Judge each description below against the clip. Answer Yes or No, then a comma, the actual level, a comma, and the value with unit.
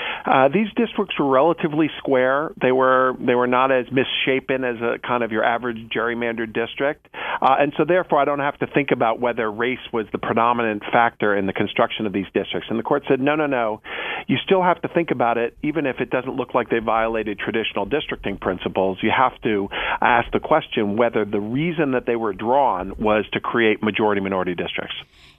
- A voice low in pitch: Yes, low, 120 Hz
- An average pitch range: Yes, average, 4.3 semitones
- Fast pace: Yes, fast, 210 wpm